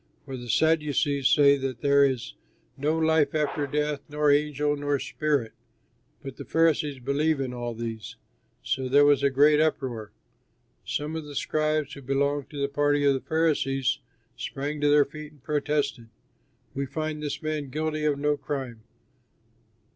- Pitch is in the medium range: Yes, medium, 145 Hz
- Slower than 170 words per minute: Yes, average, 160 wpm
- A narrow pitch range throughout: Yes, narrow, 1.9 semitones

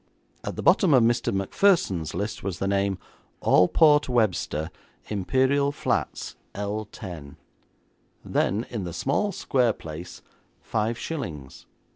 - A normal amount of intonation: No, wide, 6.3 semitones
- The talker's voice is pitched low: Yes, low, 105 Hz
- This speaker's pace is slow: Yes, slow, 115 wpm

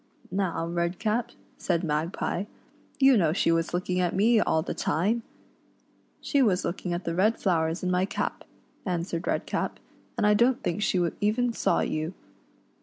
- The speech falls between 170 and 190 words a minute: Yes, average, 180 wpm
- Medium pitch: Yes, medium, 180 Hz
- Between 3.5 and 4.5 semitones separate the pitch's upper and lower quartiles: Yes, average, 3.9 semitones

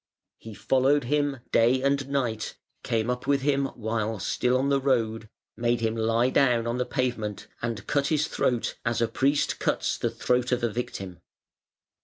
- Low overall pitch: Yes, low, 125 Hz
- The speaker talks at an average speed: Yes, average, 175 wpm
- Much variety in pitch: No, average, 3.2 semitones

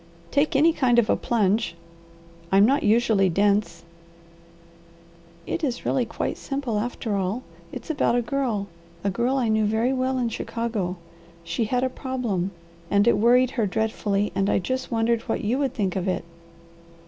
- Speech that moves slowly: No, average, 170 wpm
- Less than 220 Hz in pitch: No, high, 230 Hz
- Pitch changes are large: No, average, 4.0 semitones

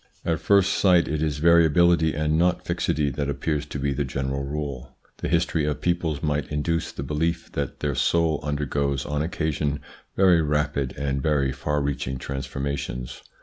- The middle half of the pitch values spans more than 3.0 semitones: No, narrow, 2.6 semitones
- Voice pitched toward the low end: Yes, very low, 75 Hz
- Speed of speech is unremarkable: Yes, average, 170 wpm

